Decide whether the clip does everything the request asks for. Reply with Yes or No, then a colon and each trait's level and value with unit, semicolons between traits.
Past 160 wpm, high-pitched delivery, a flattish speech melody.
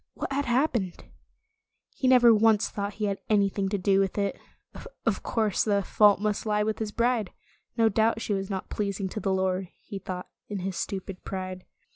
Yes: average, 195 wpm; high, 205 Hz; narrow, 2.2 semitones